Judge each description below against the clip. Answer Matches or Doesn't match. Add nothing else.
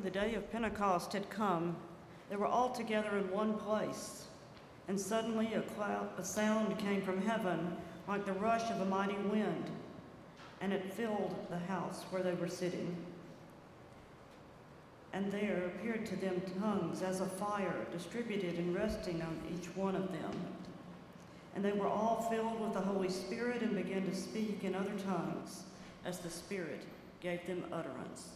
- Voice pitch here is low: Doesn't match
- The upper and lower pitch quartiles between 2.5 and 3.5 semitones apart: Matches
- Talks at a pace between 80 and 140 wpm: Doesn't match